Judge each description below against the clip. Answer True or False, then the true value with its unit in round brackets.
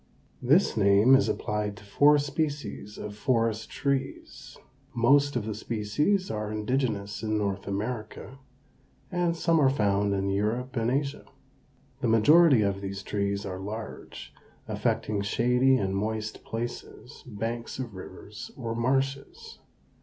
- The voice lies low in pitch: True (115 Hz)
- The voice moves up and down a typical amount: True (4.5 semitones)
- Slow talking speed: True (130 wpm)